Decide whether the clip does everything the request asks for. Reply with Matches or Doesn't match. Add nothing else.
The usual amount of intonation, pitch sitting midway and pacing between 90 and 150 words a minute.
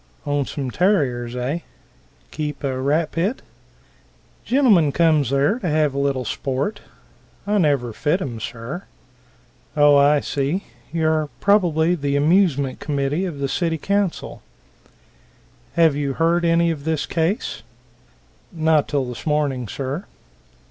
Matches